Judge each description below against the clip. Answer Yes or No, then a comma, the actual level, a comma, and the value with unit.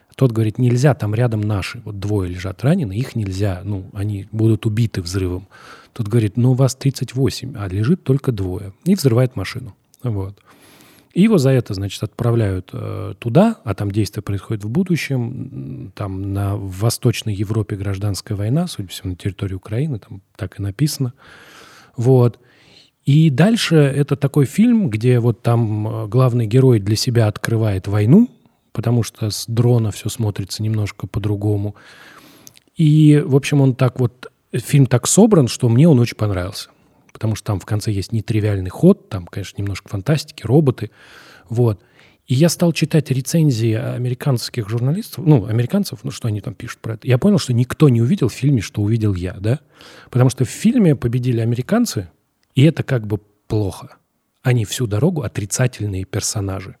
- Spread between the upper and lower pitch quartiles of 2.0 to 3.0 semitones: No, average, 4.2 semitones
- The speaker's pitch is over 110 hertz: Yes, low, 120 Hz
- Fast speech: Yes, fast, 165 wpm